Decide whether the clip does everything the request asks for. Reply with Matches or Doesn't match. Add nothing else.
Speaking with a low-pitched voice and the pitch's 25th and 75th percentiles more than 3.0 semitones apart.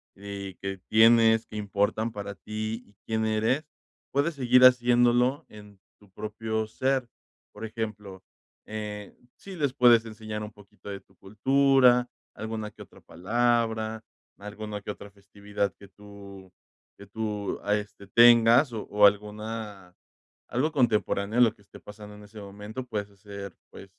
Doesn't match